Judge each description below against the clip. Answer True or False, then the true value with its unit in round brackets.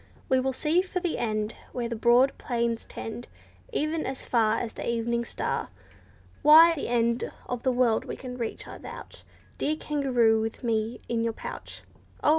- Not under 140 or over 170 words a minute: False (180 wpm)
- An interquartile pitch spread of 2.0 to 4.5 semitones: True (2.9 semitones)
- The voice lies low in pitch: False (240 Hz)